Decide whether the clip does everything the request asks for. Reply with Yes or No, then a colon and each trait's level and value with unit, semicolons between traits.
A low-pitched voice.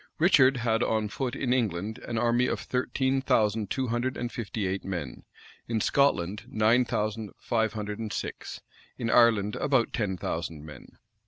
Yes: low, 115 Hz